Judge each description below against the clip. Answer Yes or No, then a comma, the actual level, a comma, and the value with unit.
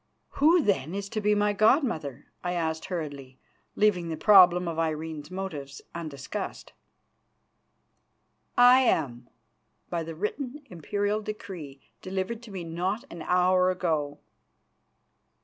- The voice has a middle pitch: Yes, medium, 180 Hz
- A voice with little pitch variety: No, average, 4.7 semitones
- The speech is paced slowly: Yes, slow, 125 wpm